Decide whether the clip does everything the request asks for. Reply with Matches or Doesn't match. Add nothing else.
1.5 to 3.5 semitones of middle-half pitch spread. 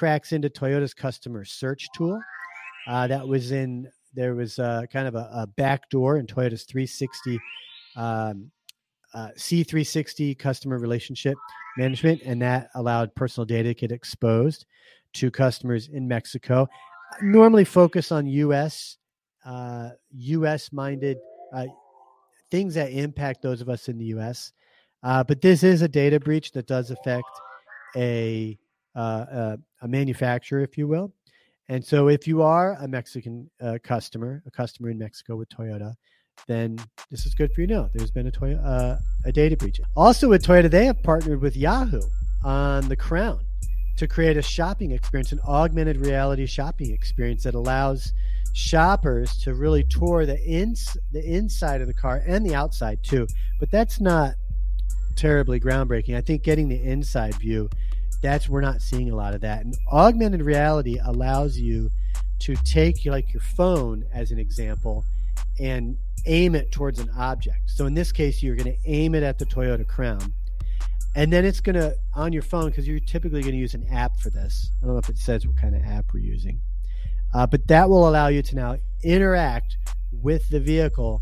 Doesn't match